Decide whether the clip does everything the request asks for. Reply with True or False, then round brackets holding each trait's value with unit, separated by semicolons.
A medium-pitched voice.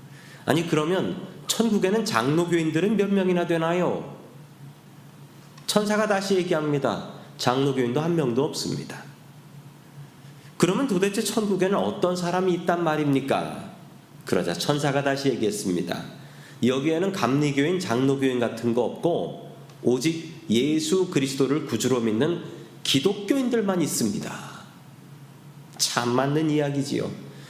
True (150 Hz)